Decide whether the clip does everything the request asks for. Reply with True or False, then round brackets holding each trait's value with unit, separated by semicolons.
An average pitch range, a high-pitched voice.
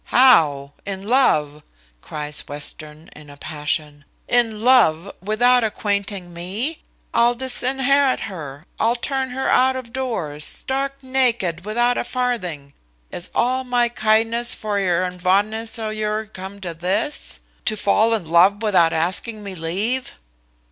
False (6.1 semitones; 210 Hz)